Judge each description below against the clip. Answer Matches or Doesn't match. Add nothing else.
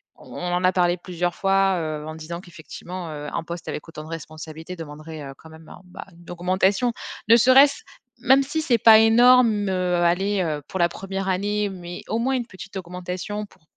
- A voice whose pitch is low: Doesn't match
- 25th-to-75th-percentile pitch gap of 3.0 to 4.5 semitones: Matches